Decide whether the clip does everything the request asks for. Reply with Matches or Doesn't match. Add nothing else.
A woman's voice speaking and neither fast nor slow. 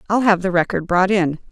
Doesn't match